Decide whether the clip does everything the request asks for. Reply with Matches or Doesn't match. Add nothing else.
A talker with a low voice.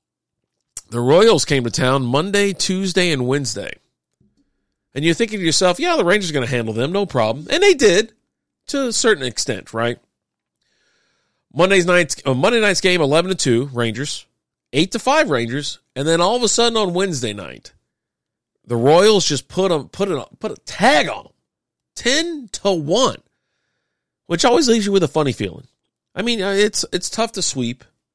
Doesn't match